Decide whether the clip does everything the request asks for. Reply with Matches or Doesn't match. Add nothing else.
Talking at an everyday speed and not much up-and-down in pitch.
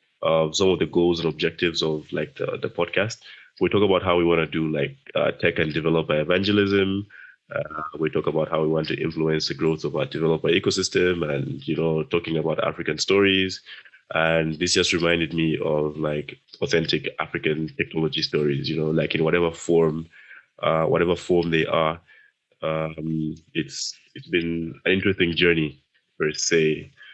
Matches